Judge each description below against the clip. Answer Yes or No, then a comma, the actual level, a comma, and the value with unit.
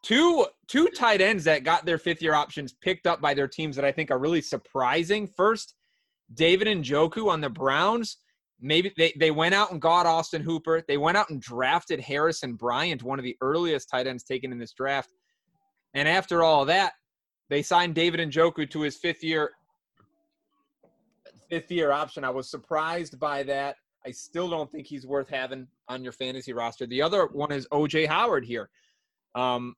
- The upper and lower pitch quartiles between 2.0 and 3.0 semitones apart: No, average, 4.1 semitones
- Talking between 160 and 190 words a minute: Yes, average, 185 wpm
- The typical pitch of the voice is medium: Yes, medium, 160 Hz